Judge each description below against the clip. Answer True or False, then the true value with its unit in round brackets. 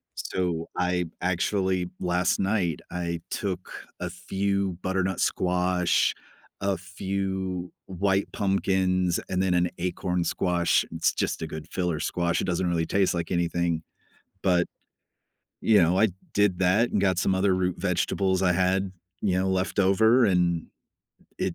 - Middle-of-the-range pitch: False (90 Hz)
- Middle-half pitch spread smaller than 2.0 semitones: True (1.5 semitones)